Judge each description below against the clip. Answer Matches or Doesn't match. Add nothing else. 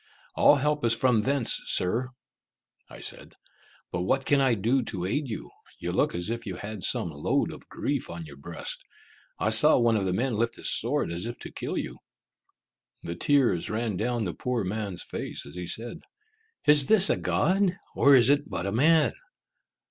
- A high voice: Doesn't match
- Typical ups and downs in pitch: Doesn't match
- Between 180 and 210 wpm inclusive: Matches